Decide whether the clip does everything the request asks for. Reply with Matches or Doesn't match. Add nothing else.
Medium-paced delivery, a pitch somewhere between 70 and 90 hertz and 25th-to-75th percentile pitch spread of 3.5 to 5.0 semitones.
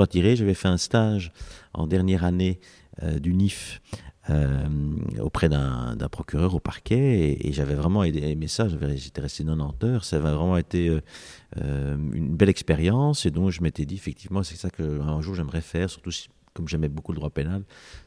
Matches